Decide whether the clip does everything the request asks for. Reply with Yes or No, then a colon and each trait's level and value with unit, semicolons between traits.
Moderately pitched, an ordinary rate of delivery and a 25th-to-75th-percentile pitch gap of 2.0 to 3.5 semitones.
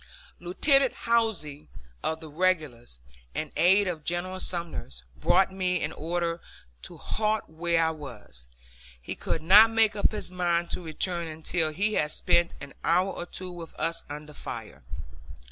Yes: medium, 170 Hz; average, 155 wpm; average, 3.1 semitones